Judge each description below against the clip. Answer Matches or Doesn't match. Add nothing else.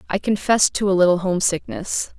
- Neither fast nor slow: Matches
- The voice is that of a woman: Matches